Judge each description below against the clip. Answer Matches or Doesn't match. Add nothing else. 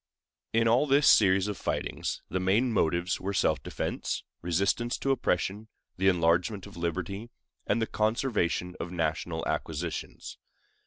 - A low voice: Matches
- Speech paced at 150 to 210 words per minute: Doesn't match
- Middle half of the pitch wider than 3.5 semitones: Matches